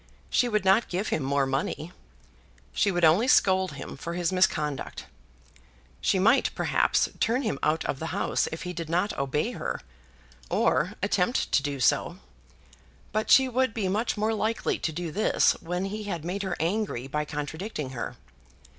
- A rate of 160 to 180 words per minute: Yes, average, 170 wpm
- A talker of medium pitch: Yes, medium, 180 Hz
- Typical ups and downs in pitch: No, wide, 5.8 semitones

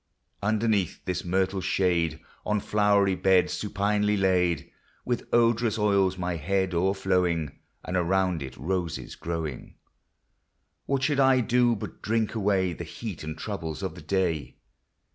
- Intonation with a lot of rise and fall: No, average, 3.2 semitones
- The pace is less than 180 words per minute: Yes, slow, 135 wpm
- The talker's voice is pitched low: Yes, very low, 95 Hz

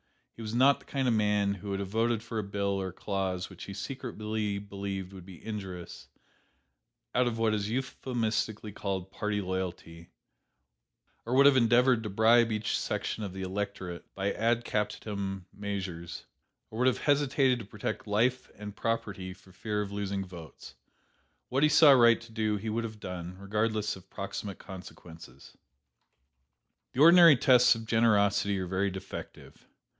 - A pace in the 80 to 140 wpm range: No, average, 165 wpm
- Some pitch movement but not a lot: Yes, average, 3.0 semitones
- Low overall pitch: Yes, low, 105 Hz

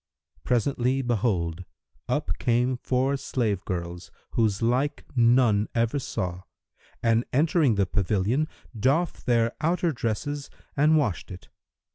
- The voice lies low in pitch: Yes, low, 120 Hz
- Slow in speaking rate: Yes, slow, 115 wpm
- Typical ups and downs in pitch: Yes, average, 4.8 semitones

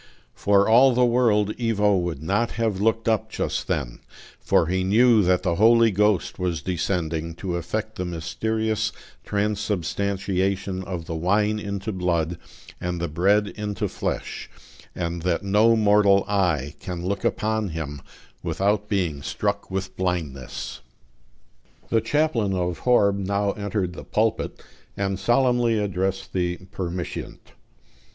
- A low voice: Yes, low, 100 Hz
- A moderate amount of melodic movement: Yes, average, 3.3 semitones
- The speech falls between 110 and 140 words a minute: Yes, slow, 135 wpm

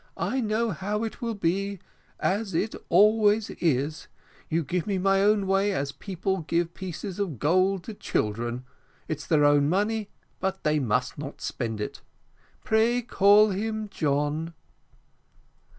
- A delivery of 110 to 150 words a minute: Yes, average, 145 wpm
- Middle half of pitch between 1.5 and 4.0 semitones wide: No, wide, 5.4 semitones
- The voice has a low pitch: No, high, 190 Hz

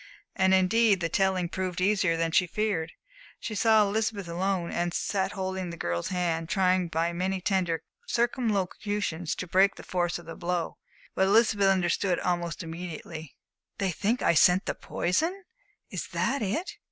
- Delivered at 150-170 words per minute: Yes, average, 160 wpm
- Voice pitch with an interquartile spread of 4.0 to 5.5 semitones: No, narrow, 2.6 semitones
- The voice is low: No, medium, 185 Hz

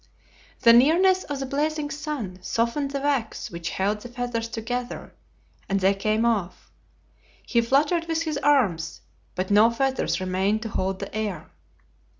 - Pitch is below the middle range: No, high, 235 Hz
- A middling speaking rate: Yes, average, 150 wpm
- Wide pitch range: Yes, wide, 5.8 semitones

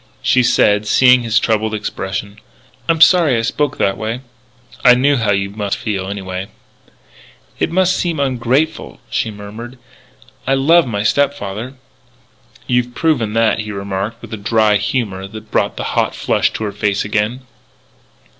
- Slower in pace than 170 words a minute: Yes, average, 155 wpm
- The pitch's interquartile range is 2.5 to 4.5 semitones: Yes, average, 3.7 semitones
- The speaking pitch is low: Yes, low, 110 Hz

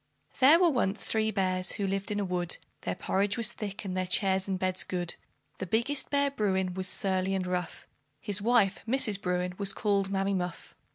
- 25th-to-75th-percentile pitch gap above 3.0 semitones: No, narrow, 2.6 semitones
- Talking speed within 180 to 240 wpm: Yes, average, 195 wpm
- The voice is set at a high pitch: Yes, high, 195 Hz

